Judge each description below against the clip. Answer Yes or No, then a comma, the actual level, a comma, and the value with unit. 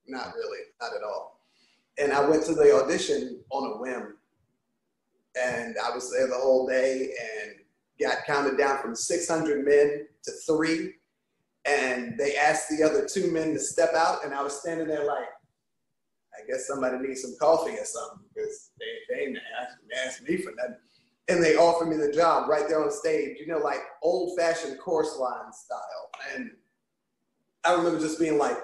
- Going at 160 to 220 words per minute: Yes, average, 180 wpm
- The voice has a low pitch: No, medium, 165 Hz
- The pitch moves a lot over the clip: Yes, wide, 6.6 semitones